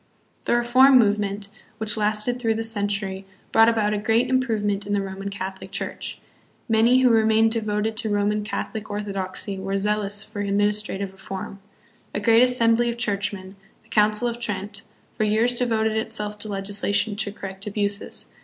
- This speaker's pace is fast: No, average, 165 wpm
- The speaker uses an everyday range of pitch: No, narrow, 1.8 semitones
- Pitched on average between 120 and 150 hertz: No, high, 210 Hz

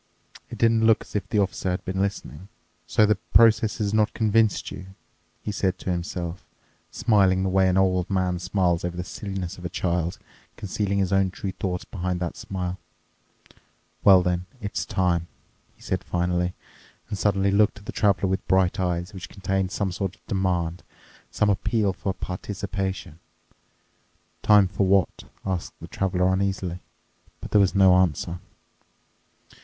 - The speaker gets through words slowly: No, average, 160 wpm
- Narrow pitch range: Yes, narrow, 1.8 semitones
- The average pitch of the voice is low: Yes, very low, 95 Hz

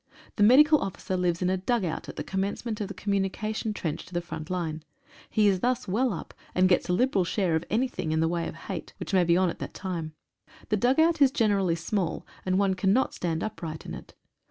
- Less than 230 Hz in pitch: Yes, high, 190 Hz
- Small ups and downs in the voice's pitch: No, average, 3.8 semitones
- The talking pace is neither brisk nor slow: No, fast, 225 wpm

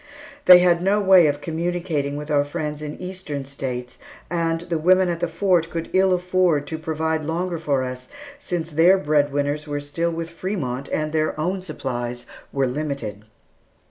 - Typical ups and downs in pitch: Yes, average, 3.5 semitones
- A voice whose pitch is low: No, medium, 160 Hz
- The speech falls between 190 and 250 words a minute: No, average, 175 wpm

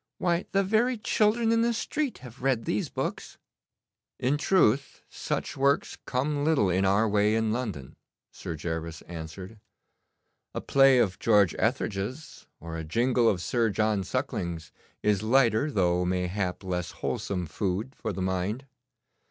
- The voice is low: Yes, low, 110 Hz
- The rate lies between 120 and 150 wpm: Yes, average, 145 wpm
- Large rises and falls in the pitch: Yes, wide, 6.9 semitones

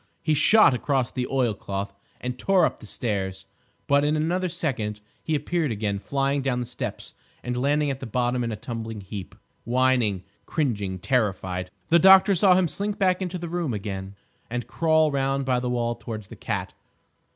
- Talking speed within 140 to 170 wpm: No, average, 180 wpm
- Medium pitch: No, low, 130 Hz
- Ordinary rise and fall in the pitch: No, wide, 6.3 semitones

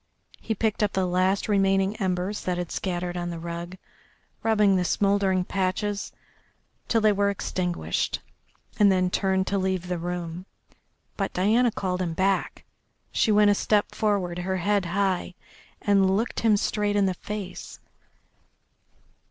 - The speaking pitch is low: No, high, 190 Hz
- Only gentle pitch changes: Yes, narrow, 2.1 semitones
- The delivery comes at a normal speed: Yes, average, 150 wpm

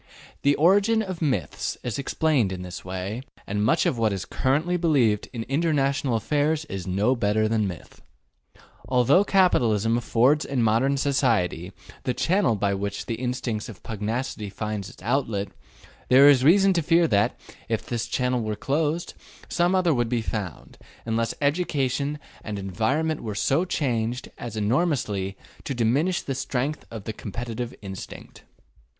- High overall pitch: No, low, 125 Hz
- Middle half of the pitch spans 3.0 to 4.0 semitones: No, average, 5.3 semitones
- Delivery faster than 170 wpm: No, average, 155 wpm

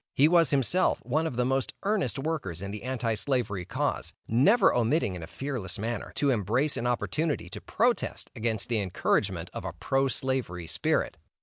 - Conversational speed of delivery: Yes, average, 180 wpm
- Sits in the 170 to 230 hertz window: No, low, 125 Hz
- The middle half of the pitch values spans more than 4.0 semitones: Yes, average, 5.2 semitones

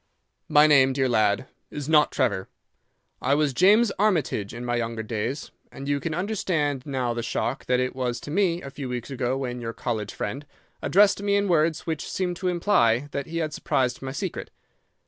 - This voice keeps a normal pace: Yes, average, 195 wpm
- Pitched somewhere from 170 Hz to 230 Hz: No, medium, 140 Hz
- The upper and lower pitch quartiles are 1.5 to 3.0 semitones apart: No, average, 5.3 semitones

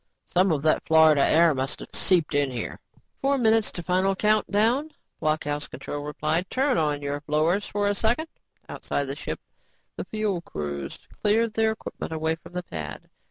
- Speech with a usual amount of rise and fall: No, wide, 6.3 semitones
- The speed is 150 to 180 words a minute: Yes, average, 170 wpm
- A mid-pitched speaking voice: Yes, medium, 170 Hz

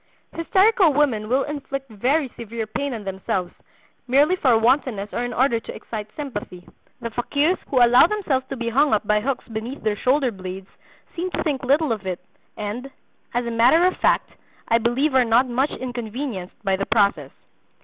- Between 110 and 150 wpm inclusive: No, average, 180 wpm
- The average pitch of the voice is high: Yes, high, 245 Hz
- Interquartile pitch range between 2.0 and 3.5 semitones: No, average, 4.5 semitones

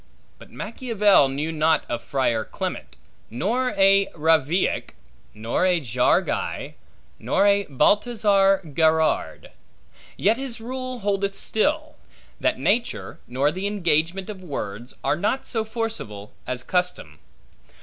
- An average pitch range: No, wide, 6.5 semitones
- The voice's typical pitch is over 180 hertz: Yes, high, 190 Hz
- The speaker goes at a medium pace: No, slow, 120 wpm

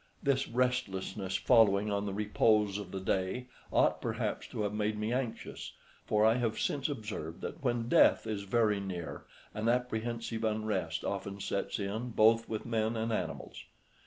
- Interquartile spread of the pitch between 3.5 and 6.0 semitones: No, average, 2.7 semitones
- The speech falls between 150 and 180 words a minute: Yes, average, 160 wpm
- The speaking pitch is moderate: No, low, 110 Hz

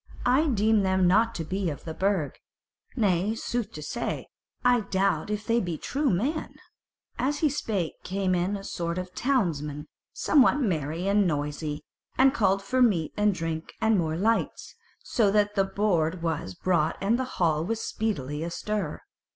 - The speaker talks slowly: No, average, 170 wpm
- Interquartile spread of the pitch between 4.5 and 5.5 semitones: Yes, average, 5.0 semitones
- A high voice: Yes, high, 195 Hz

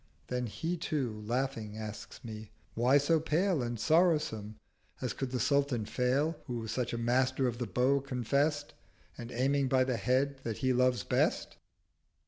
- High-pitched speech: No, low, 130 Hz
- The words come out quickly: No, average, 165 wpm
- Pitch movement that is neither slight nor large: Yes, average, 3.1 semitones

